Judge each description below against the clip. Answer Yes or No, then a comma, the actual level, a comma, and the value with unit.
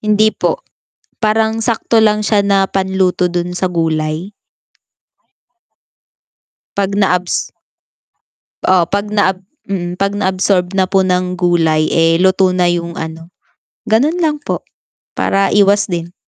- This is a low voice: No, high, 190 Hz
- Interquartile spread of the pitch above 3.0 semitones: No, narrow, 2.6 semitones